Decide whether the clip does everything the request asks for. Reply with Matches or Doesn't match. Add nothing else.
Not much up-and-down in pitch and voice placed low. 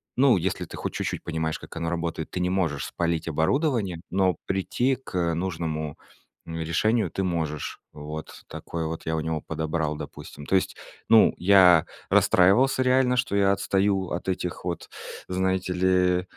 Doesn't match